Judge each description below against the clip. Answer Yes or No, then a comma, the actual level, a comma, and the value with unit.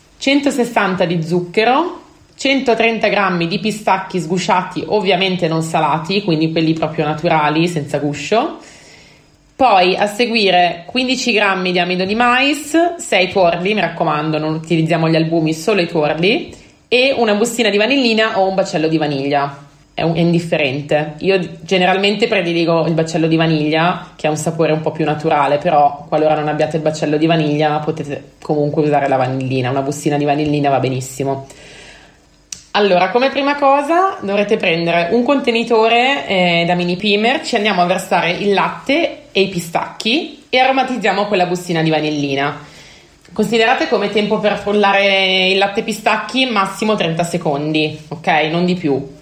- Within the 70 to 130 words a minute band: No, average, 155 wpm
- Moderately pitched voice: Yes, medium, 180 Hz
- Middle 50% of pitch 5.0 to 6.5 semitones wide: Yes, wide, 5.6 semitones